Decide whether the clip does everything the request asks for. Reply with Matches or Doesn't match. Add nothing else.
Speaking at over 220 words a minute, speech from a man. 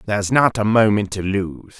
Doesn't match